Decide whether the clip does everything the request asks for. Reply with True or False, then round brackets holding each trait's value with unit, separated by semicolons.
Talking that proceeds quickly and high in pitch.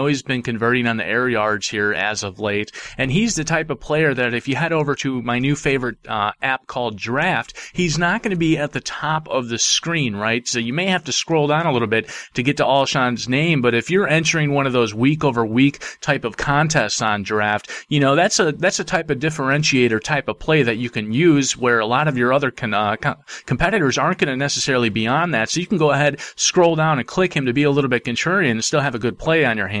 False (260 wpm; 135 Hz)